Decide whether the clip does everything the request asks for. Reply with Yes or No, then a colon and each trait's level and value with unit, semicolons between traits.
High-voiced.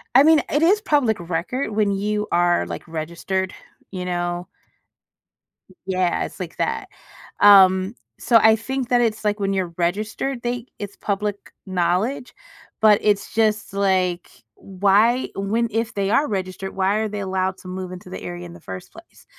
Yes: high, 200 Hz